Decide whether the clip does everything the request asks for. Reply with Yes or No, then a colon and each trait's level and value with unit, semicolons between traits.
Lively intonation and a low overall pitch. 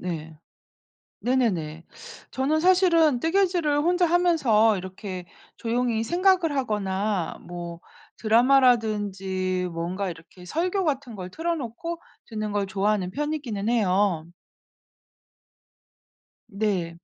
No: wide, 8.0 semitones; high, 220 Hz